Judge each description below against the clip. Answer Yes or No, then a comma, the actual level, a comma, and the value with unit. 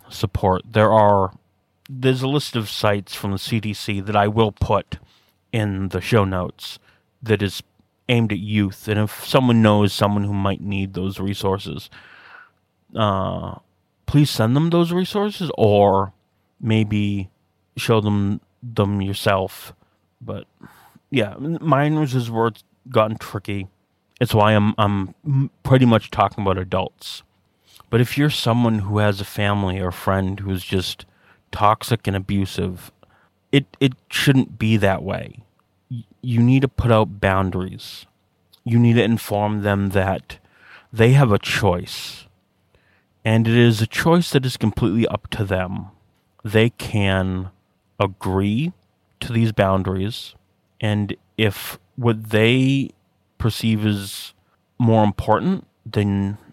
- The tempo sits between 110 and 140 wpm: Yes, slow, 135 wpm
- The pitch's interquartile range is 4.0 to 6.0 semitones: No, average, 3.3 semitones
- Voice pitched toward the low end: Yes, low, 105 Hz